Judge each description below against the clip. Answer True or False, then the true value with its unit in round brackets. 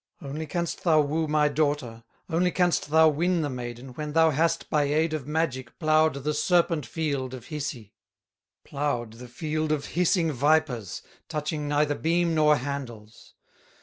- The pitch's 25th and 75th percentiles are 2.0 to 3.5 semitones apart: True (2.8 semitones)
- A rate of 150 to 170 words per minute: True (155 wpm)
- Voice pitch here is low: False (150 Hz)